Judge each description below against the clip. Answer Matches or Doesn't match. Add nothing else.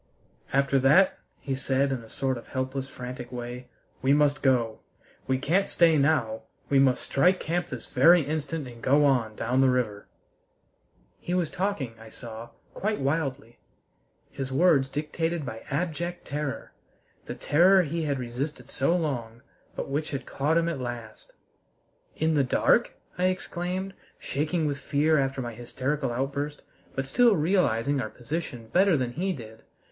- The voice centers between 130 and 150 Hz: Matches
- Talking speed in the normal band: Matches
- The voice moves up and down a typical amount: Matches